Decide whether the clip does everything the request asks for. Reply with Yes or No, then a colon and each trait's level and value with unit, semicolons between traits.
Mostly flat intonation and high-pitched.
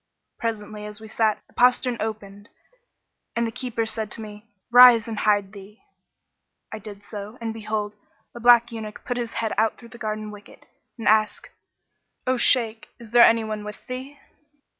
Yes: narrow, 1.9 semitones; high, 220 Hz